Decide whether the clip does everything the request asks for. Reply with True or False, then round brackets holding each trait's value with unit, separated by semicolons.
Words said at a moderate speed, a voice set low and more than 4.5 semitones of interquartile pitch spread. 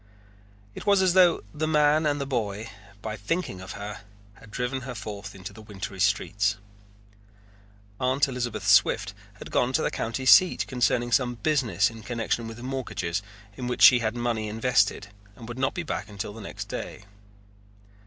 False (175 wpm; 120 Hz; 4.1 semitones)